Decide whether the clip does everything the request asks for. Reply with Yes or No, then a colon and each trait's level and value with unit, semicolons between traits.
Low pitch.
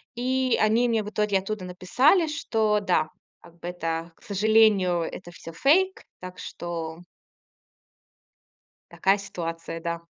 No: high, 195 Hz